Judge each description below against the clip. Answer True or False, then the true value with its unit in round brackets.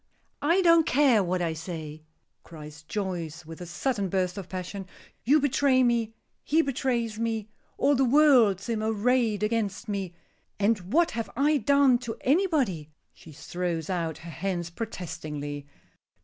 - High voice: True (210 Hz)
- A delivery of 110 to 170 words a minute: True (150 wpm)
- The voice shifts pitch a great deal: True (6.9 semitones)